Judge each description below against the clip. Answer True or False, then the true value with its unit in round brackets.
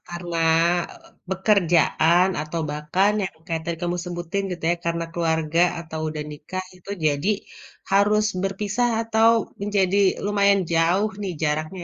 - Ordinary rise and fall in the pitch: True (3.3 semitones)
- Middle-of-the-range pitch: True (175 Hz)